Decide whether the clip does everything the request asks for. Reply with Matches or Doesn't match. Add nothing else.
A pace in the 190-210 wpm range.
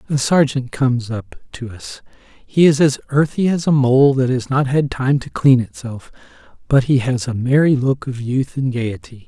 Matches